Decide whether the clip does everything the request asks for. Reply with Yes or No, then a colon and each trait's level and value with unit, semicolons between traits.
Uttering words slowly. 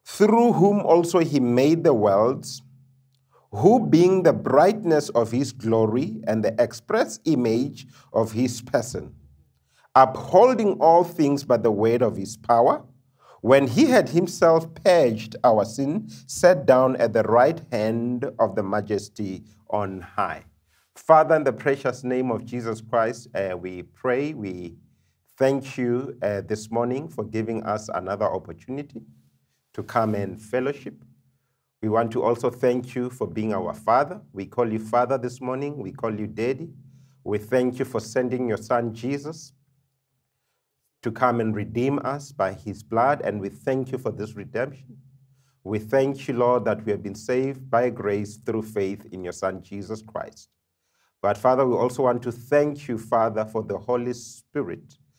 No: average, 160 wpm